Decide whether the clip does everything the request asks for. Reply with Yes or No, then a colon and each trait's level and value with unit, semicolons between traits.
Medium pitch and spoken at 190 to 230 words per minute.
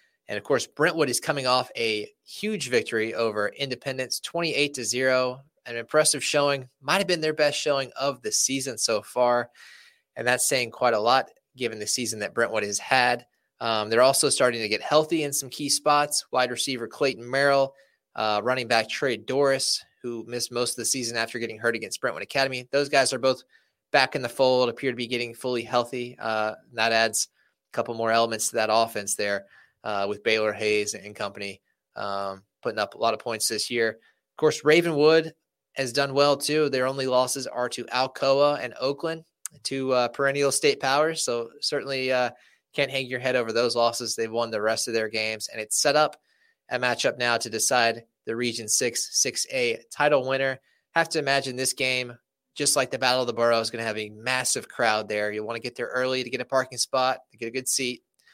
No: low, 125 Hz; fast, 205 wpm